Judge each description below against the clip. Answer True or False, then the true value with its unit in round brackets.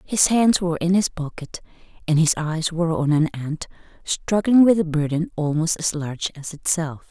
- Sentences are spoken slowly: False (185 wpm)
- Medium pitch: True (165 Hz)